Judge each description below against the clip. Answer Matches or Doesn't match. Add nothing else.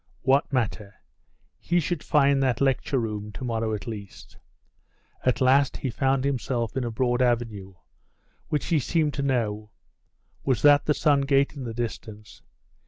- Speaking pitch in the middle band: Doesn't match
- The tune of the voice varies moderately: Matches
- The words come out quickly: Doesn't match